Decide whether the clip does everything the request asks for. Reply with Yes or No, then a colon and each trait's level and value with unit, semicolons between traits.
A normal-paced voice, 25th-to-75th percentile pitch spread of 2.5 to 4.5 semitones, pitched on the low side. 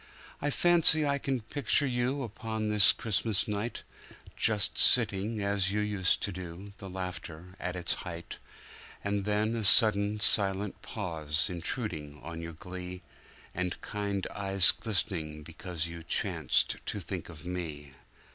No: slow, 130 wpm; average, 3.6 semitones; low, 100 Hz